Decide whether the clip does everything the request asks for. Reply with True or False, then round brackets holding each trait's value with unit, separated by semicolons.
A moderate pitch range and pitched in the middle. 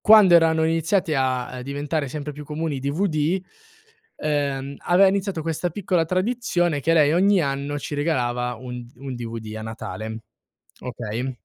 True (4.7 semitones; 150 Hz)